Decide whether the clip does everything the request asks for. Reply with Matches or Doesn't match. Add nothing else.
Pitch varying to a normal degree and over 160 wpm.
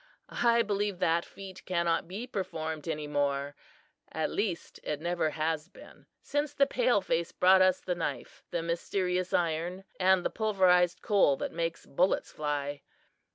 Doesn't match